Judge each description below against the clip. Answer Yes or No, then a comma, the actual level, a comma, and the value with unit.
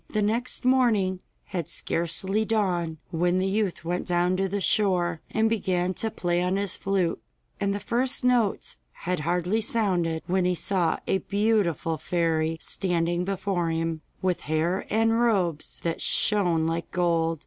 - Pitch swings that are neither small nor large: Yes, average, 3.3 semitones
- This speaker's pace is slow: No, average, 155 wpm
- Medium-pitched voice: Yes, medium, 180 Hz